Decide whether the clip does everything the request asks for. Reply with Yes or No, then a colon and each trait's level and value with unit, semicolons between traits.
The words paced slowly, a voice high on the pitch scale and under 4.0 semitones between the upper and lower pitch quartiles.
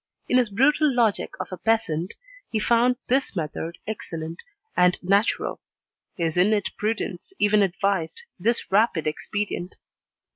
No: slow, 125 wpm; high, 205 Hz; average, 4.3 semitones